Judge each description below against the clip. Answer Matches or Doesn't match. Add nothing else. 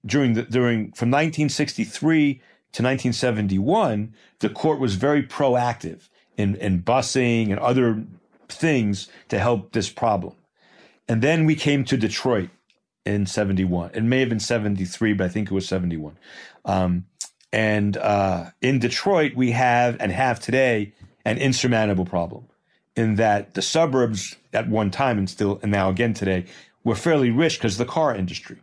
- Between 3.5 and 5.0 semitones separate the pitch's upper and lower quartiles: Matches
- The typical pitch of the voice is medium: Doesn't match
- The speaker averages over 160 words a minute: Doesn't match